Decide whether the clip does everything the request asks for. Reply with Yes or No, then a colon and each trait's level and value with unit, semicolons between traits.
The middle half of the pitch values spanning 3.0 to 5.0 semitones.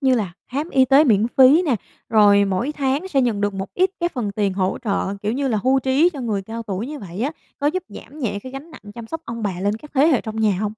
No: wide, 5.4 semitones